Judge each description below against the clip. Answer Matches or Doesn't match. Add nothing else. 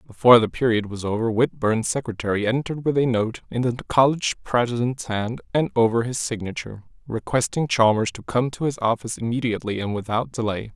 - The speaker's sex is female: Doesn't match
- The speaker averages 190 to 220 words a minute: Doesn't match